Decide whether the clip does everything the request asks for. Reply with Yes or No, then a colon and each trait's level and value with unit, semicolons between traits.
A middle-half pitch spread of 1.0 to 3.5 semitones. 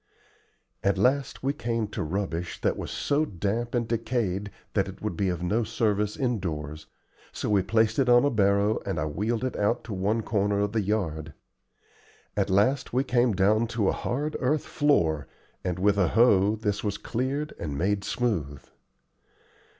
No: average, 3.9 semitones